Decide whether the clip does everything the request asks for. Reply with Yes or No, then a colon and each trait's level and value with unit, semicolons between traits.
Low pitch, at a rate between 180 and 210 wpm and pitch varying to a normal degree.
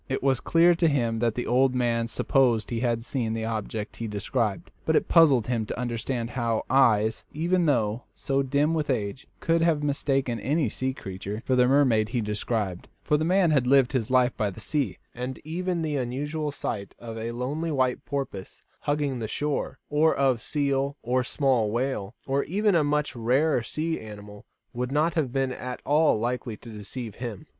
Yes: low, 130 Hz; average, 190 wpm; average, 4.1 semitones